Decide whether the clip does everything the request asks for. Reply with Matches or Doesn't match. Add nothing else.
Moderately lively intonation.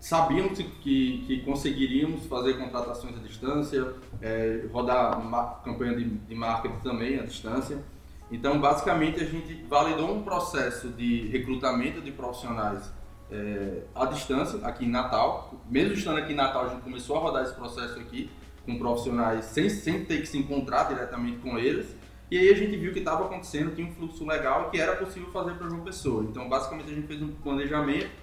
Matches